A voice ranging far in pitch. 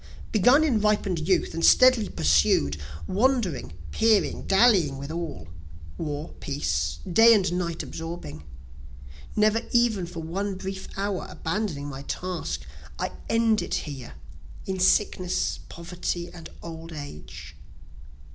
Yes: wide, 5.8 semitones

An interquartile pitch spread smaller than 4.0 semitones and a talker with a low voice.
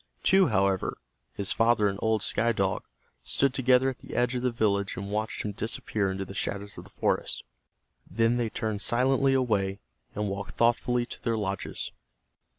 Yes: average, 3.5 semitones; low, 110 Hz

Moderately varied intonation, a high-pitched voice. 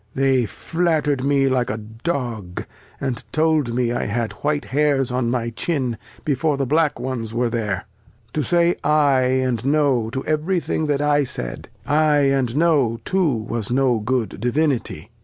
No: average, 4.0 semitones; low, 130 Hz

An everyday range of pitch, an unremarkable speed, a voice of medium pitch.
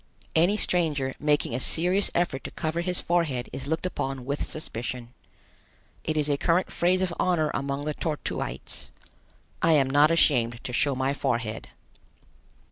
Yes: average, 4.1 semitones; average, 160 wpm; medium, 150 Hz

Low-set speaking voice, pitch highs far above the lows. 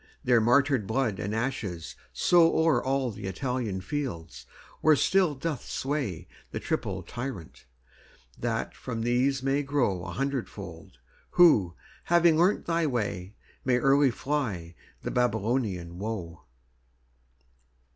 Yes: low, 125 Hz; wide, 6.1 semitones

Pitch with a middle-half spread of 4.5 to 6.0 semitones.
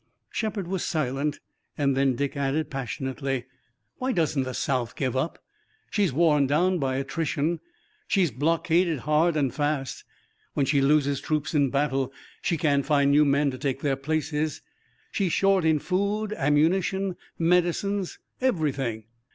No: average, 3.8 semitones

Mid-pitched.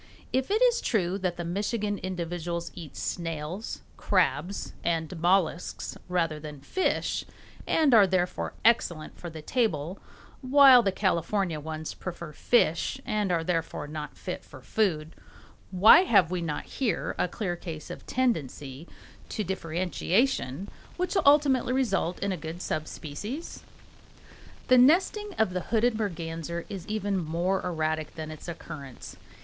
Yes: medium, 180 Hz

